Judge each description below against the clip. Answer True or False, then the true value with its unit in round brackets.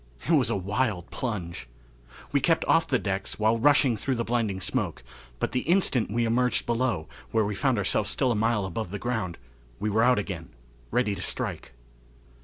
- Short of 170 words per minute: False (190 wpm)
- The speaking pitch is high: False (110 Hz)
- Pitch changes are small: False (4.0 semitones)